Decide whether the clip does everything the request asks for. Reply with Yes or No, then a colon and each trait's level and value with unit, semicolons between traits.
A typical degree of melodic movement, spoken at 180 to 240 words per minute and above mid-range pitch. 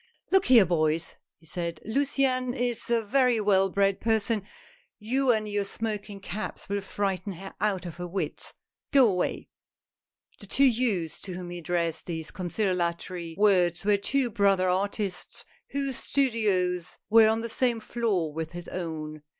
No: average, 4.3 semitones; average, 165 wpm; high, 200 Hz